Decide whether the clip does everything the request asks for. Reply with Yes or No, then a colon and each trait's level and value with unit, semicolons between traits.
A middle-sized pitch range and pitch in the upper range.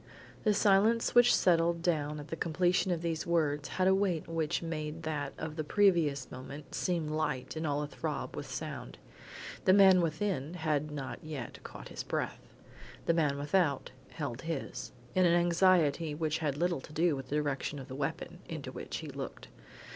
No: average, 3.0 semitones; medium, 160 Hz